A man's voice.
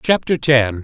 Yes: male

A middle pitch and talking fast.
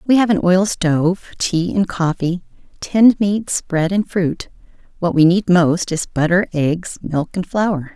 No: medium, 180 Hz; average, 175 wpm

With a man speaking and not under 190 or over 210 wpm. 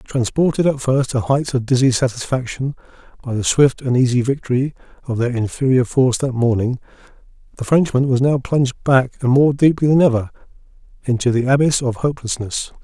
No: male; average, 170 wpm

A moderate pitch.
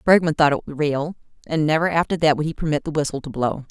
Yes: medium, 150 Hz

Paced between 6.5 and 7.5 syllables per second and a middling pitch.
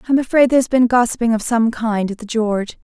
No: 6.8 syllables/s; high, 230 Hz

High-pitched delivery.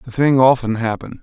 No: low, 125 Hz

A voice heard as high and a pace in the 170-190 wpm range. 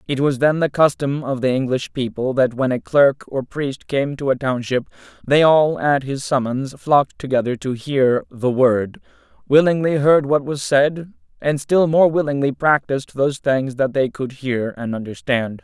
No: low, 135 Hz; average, 185 wpm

